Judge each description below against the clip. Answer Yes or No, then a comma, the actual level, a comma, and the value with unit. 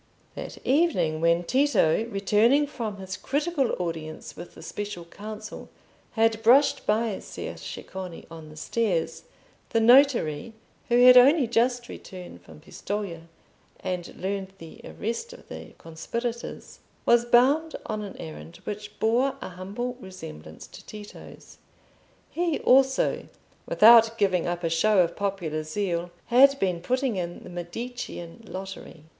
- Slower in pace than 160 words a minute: Yes, slow, 135 wpm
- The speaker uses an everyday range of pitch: No, wide, 5.8 semitones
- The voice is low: No, high, 205 Hz